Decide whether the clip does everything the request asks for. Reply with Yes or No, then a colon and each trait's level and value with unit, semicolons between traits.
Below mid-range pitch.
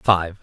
Yes: very low, 90 Hz